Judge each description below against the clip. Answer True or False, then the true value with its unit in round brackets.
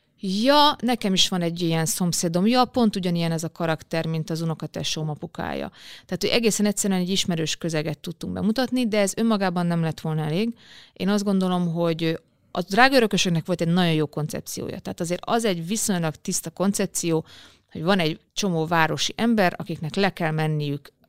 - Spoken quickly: True (175 wpm)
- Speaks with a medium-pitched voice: True (180 Hz)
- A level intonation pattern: False (3.9 semitones)